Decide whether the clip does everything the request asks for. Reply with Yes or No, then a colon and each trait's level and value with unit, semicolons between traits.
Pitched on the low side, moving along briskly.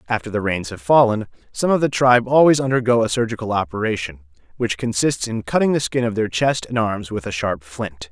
Yes: low, 110 Hz; fast, 215 wpm